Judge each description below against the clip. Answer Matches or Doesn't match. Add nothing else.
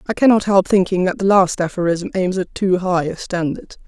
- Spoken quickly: Matches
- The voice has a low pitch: Doesn't match